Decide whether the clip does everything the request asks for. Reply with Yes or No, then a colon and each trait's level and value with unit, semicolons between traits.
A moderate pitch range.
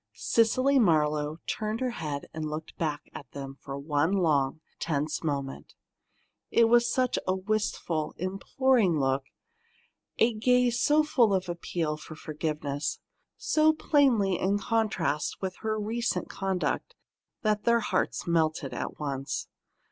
No: wide, 7.0 semitones